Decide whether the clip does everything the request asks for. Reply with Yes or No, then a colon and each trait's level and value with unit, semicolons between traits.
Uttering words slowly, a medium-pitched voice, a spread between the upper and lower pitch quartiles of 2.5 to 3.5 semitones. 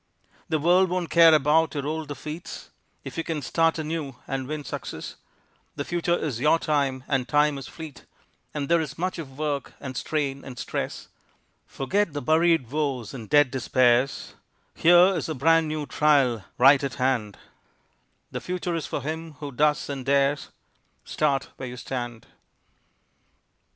No: average, 160 wpm; medium, 150 Hz; average, 3.1 semitones